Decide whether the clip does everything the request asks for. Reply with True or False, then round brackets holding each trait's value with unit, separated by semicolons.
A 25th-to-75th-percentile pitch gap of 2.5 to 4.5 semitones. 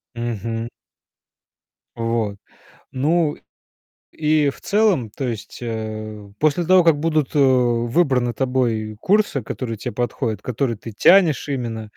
False (5.1 semitones)